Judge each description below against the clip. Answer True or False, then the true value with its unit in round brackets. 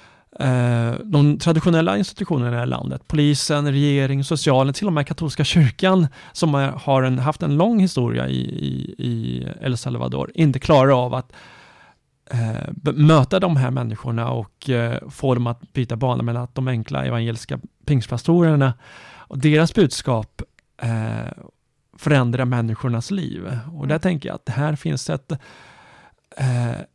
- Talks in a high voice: False (135 Hz)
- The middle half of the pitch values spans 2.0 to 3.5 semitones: False (4.3 semitones)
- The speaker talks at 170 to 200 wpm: False (145 wpm)